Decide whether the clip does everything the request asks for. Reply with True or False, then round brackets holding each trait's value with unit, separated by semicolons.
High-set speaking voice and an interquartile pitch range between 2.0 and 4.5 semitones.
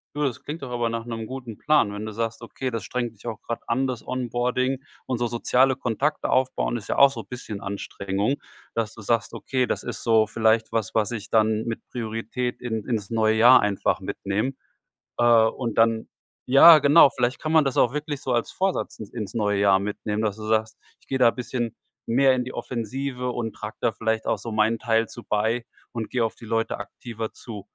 False (115 Hz; 2.5 semitones)